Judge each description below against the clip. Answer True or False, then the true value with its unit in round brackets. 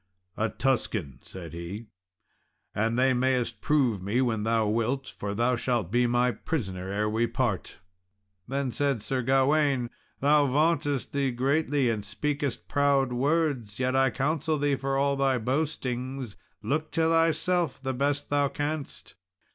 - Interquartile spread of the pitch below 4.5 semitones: True (3.7 semitones)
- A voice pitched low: True (130 Hz)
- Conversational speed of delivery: True (145 wpm)